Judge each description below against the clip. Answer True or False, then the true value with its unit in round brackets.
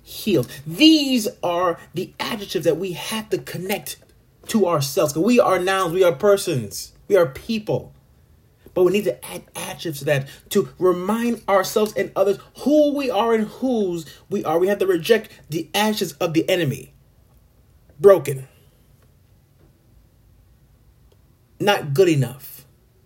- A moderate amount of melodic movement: False (7.7 semitones)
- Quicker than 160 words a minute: False (140 wpm)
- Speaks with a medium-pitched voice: True (175 Hz)